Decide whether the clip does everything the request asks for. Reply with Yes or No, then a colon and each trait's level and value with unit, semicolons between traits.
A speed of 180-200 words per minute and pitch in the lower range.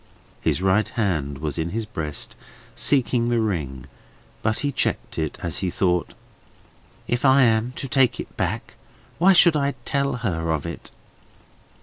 No: average, 155 wpm; low, 110 Hz